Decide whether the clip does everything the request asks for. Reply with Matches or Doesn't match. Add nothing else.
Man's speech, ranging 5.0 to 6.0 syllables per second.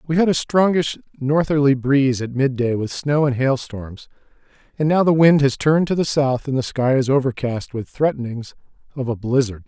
Matches